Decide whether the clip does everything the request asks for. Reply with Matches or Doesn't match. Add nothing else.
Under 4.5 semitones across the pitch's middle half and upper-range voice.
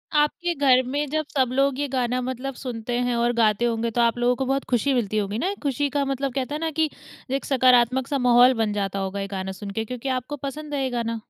Matches